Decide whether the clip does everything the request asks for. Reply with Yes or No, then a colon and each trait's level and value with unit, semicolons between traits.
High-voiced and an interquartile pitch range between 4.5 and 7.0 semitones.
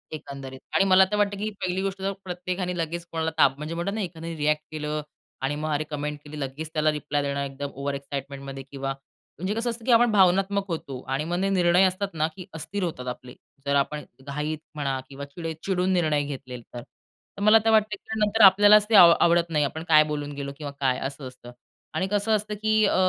No: medium, 160 Hz; average, 5.3 semitones